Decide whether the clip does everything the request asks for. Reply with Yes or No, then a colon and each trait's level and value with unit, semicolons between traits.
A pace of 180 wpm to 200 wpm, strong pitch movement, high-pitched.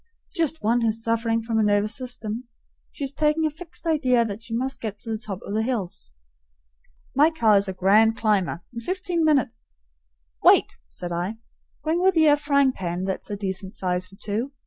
Yes: average, 195 wpm; wide, 6.0 semitones; high, 225 Hz